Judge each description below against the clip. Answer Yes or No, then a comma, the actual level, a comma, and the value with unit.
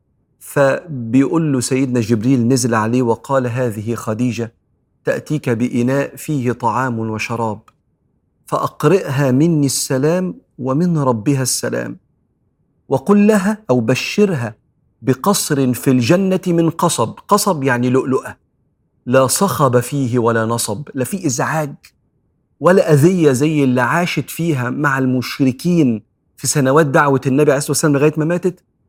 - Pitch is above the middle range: No, low, 135 Hz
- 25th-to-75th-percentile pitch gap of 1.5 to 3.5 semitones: No, average, 4.0 semitones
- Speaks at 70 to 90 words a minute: No, average, 120 wpm